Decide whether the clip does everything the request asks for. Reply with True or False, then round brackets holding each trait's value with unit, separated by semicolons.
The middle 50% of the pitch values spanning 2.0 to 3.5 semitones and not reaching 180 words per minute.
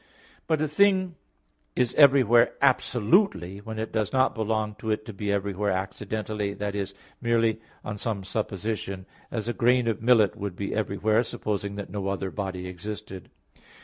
True (2.8 semitones; 160 wpm)